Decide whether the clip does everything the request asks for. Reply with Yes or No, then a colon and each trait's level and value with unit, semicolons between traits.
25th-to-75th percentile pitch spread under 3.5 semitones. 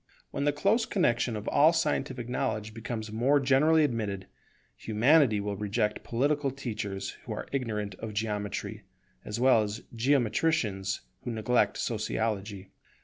No: average, 4.6 semitones